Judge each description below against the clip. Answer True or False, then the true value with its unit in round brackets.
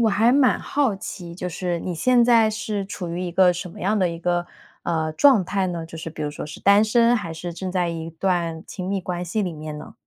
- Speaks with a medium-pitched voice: True (180 Hz)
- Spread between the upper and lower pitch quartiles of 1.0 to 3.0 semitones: False (3.7 semitones)